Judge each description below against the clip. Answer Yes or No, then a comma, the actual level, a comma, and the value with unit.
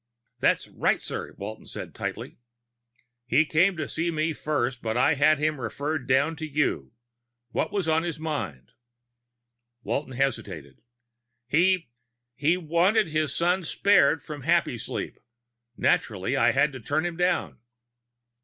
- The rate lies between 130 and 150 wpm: Yes, slow, 135 wpm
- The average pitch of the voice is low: No, medium, 155 Hz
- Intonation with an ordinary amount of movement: Yes, average, 3.8 semitones